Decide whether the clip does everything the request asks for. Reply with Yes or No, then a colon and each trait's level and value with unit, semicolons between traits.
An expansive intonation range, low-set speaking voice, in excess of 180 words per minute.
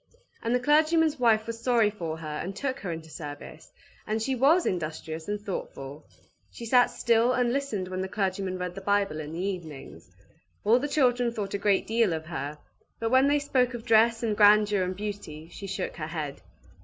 No: wide, 5.9 semitones; high, 205 Hz; average, 200 wpm